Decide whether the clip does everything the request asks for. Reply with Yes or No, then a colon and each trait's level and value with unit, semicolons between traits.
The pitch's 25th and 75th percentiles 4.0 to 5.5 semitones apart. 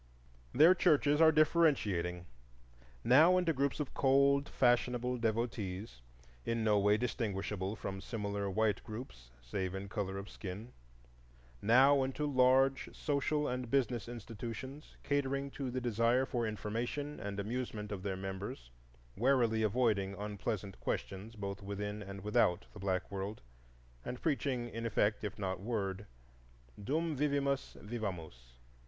Yes: average, 5.1 semitones